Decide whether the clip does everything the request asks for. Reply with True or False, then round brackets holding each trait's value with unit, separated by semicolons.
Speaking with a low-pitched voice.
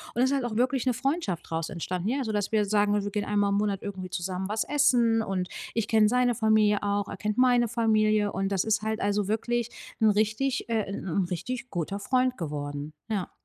False (210 Hz)